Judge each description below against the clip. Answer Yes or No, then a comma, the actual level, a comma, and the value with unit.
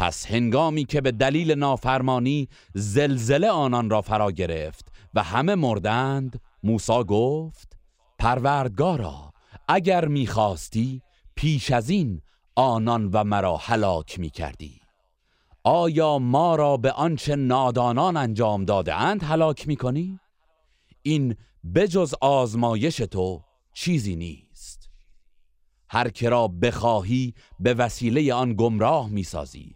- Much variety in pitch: Yes, wide, 5.8 semitones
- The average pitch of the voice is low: Yes, low, 120 Hz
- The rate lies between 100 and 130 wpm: Yes, average, 115 wpm